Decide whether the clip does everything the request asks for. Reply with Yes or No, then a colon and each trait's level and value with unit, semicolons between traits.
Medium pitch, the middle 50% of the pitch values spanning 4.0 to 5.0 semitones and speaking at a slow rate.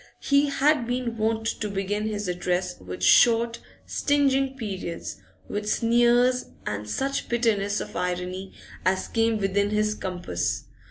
No: high, 215 Hz; average, 4.3 semitones; slow, 130 wpm